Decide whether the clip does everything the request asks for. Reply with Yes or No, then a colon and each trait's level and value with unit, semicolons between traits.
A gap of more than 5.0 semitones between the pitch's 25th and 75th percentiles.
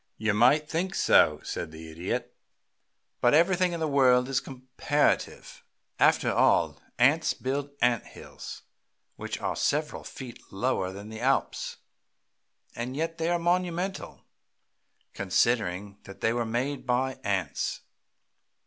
Yes: wide, 5.6 semitones